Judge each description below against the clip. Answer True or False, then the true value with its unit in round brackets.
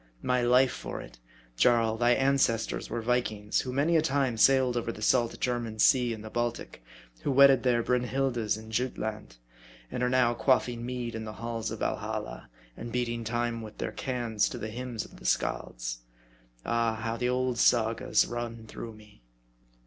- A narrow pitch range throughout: True (2.0 semitones)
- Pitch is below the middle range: True (120 Hz)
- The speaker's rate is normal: True (180 wpm)